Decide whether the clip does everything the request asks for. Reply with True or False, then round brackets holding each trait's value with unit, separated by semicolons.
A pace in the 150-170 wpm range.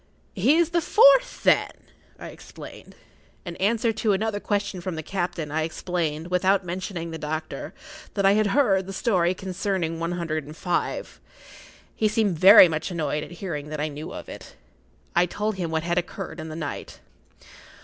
False (180 wpm)